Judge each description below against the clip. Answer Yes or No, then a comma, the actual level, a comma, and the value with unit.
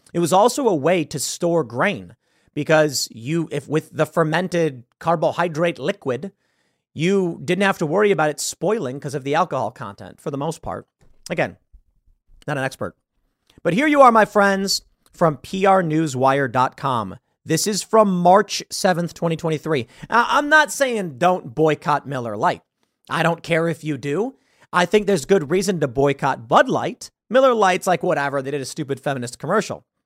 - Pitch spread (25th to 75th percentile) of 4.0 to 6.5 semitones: Yes, average, 4.9 semitones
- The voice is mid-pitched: Yes, medium, 165 Hz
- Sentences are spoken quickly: No, average, 170 wpm